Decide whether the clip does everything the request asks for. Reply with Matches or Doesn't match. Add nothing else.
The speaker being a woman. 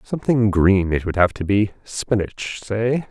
Doesn't match